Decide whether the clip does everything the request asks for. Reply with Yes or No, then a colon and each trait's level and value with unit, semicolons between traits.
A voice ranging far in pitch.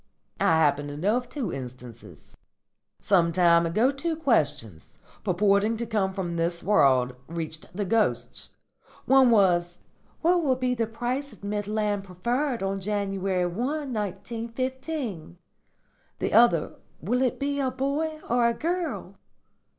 Yes: wide, 6.6 semitones